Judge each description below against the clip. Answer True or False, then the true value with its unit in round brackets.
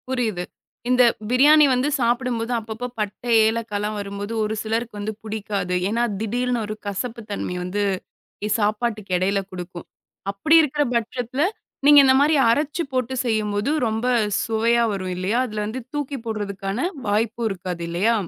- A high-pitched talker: True (220 Hz)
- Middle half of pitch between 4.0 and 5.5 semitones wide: False (3.4 semitones)